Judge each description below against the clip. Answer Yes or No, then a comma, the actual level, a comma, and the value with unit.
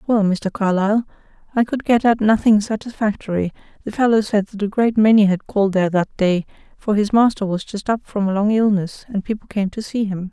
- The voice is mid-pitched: No, high, 210 Hz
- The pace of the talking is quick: Yes, fast, 215 wpm